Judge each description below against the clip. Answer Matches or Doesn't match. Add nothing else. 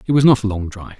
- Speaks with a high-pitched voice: Doesn't match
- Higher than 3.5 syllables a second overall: Matches